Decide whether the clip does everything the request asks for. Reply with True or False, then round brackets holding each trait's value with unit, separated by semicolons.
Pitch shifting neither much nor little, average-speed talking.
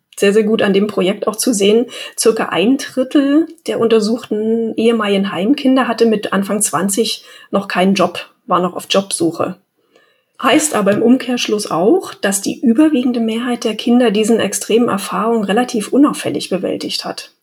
True (3.6 semitones; 155 wpm)